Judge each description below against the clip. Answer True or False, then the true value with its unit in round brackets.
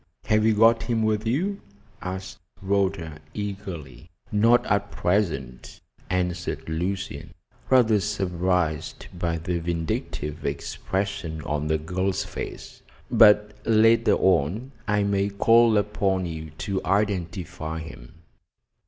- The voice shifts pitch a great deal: False (4.2 semitones)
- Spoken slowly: True (110 wpm)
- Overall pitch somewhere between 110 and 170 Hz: False (95 Hz)